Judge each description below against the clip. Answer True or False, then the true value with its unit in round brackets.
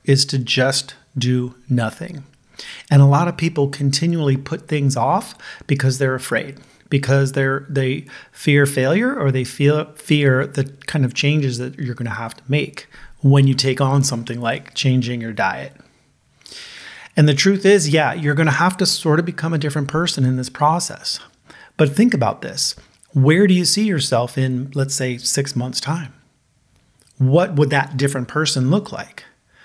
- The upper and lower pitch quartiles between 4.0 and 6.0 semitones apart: False (2.8 semitones)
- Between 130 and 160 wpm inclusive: False (175 wpm)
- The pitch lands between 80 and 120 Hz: False (140 Hz)